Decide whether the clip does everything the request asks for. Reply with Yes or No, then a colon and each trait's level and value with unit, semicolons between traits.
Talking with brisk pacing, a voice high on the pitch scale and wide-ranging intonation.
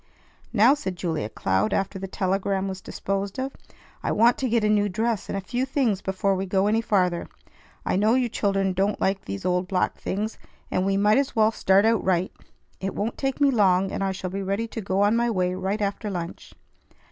No: fast, 215 wpm; high, 195 Hz; average, 2.8 semitones